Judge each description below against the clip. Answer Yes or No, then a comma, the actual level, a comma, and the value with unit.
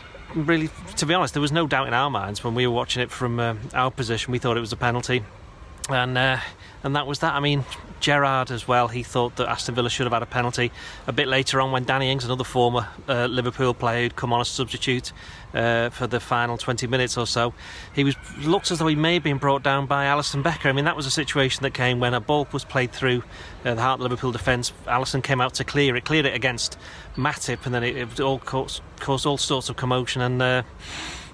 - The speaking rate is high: Yes, fast, 245 wpm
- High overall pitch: No, low, 125 Hz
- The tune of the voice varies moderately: No, narrow, 2.3 semitones